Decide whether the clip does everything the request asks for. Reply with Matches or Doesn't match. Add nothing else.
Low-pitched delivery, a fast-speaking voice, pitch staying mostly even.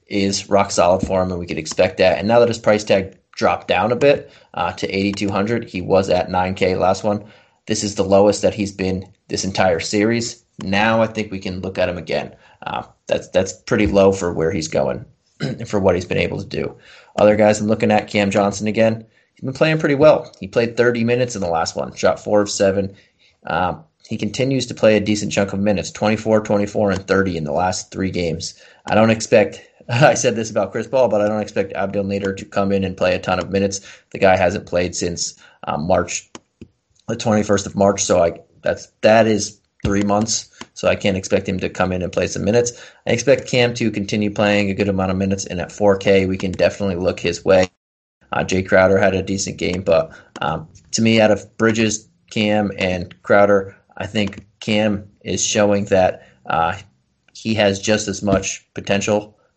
Matches